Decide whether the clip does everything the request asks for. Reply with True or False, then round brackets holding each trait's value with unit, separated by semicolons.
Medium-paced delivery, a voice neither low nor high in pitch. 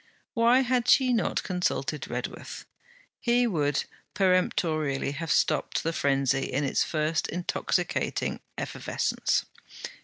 False (110 wpm; 165 Hz)